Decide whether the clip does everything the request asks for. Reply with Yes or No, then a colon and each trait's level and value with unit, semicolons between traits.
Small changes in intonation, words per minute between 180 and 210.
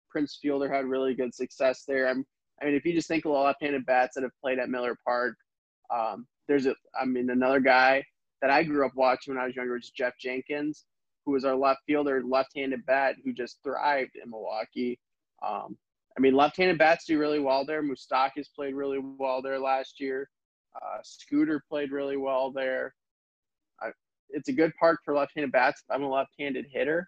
Yes: narrow, 2.0 semitones; average, 200 wpm